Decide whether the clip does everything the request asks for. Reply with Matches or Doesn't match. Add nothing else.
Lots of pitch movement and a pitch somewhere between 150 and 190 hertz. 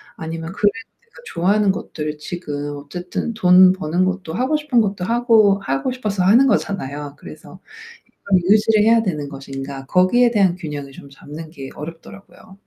Matches